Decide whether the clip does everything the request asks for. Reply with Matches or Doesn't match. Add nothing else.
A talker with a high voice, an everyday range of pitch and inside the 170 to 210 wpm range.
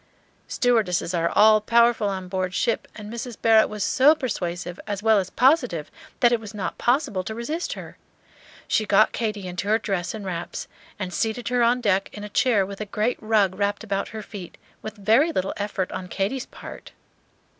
Matches